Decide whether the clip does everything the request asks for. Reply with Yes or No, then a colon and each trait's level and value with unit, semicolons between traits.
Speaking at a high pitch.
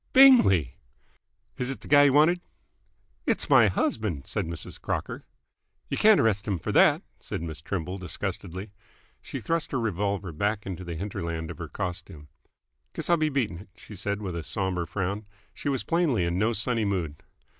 No: low, 100 Hz